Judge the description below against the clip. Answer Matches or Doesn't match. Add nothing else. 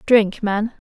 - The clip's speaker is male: Doesn't match